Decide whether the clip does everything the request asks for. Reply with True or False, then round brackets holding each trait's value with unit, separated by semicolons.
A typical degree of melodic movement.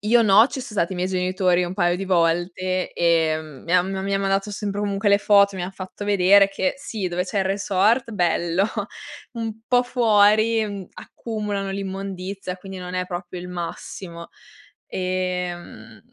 False (2.2 semitones)